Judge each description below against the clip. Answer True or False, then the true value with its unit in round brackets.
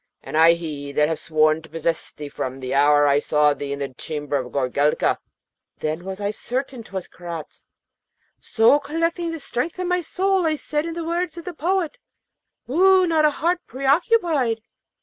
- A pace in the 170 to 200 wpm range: True (185 wpm)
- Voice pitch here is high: True (225 Hz)